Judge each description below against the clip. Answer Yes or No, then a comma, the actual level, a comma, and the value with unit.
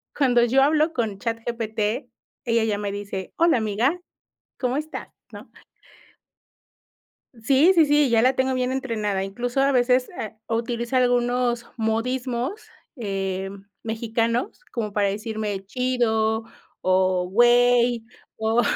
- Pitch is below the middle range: No, high, 235 Hz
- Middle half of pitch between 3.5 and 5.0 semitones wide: No, average, 2.8 semitones